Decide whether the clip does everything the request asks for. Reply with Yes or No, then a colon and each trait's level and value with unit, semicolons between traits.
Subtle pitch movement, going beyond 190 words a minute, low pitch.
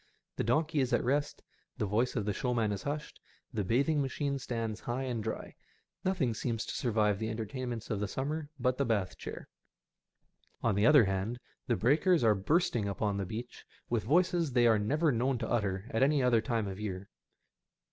No: average, 4.4 semitones; average, 200 wpm; low, 120 Hz